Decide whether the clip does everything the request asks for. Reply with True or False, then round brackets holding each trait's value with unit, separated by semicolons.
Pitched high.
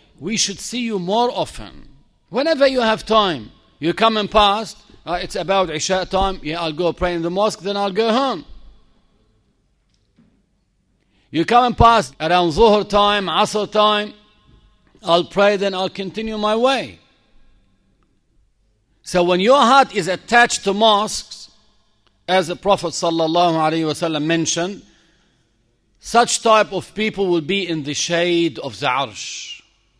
True (195 Hz)